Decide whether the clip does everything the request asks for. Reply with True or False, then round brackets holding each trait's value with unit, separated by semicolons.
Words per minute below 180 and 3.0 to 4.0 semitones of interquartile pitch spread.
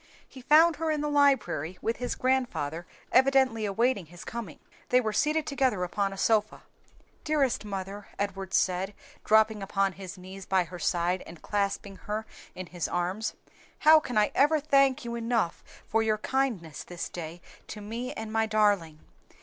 False (165 wpm; 5.4 semitones)